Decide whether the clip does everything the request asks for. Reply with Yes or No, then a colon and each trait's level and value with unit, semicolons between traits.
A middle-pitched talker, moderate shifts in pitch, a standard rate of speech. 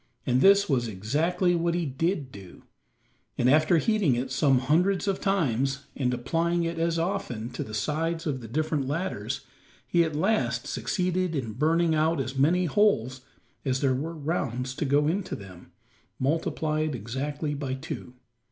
Yes: medium, 150 Hz; average, 4.6 semitones; average, 160 wpm